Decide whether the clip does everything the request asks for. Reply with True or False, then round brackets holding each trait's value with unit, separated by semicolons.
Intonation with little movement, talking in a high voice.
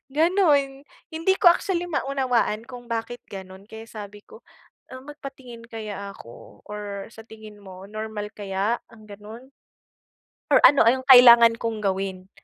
False (4.2 semitones; 225 Hz)